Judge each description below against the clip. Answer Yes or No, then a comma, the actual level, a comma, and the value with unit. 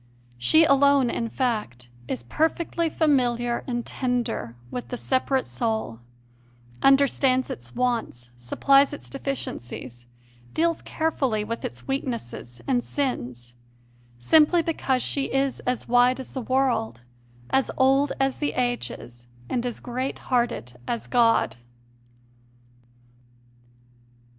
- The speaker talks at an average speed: No, slow, 115 wpm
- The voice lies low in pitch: No, very high, 250 Hz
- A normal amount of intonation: Yes, average, 3.9 semitones